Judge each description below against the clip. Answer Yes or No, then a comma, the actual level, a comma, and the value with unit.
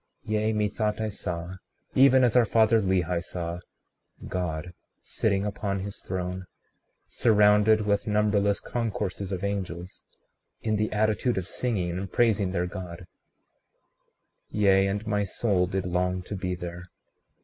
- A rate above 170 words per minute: No, average, 140 wpm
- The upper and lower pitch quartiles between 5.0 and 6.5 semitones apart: No, average, 2.9 semitones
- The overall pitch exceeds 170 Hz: No, low, 100 Hz